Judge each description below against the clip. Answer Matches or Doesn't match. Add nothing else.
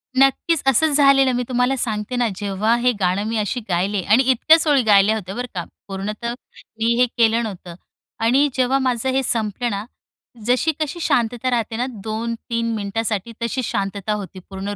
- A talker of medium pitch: Doesn't match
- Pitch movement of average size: Matches